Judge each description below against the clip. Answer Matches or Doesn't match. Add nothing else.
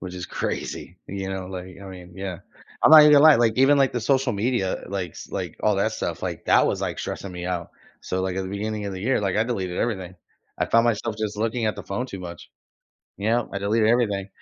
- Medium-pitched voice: Doesn't match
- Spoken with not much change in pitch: Doesn't match